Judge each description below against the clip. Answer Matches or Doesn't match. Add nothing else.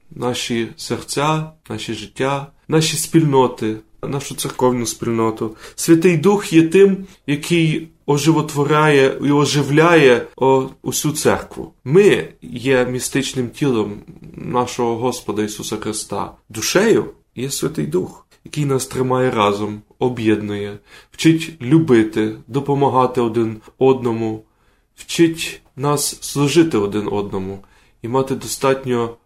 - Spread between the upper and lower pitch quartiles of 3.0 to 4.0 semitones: Doesn't match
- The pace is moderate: Doesn't match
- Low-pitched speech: Matches